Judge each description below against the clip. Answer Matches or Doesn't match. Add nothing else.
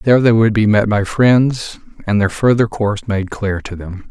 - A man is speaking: Matches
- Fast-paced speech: Matches